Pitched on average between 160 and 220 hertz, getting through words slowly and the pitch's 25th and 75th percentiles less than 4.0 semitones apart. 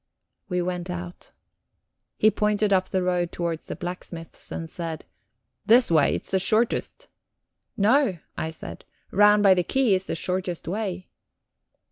No: medium, 185 Hz; average, 145 wpm; average, 3.0 semitones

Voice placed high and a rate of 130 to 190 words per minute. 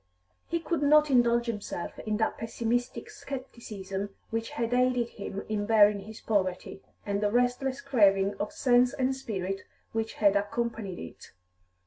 Yes: high, 225 Hz; average, 145 wpm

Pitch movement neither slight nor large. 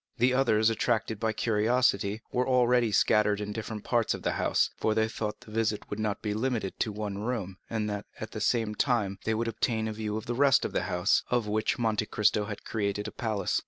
No: narrow, 1.9 semitones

